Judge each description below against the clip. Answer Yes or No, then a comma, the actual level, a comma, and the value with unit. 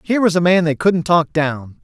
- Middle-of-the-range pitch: Yes, medium, 170 Hz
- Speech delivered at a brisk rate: Yes, fast, 260 wpm